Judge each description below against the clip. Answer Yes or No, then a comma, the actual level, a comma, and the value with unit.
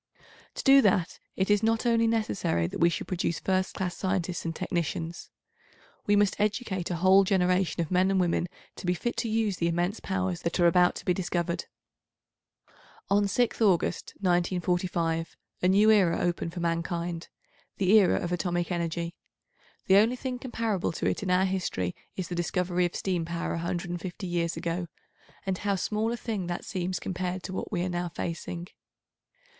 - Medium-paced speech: Yes, average, 175 wpm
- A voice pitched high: No, medium, 180 Hz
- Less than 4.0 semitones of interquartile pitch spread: Yes, narrow, 2.4 semitones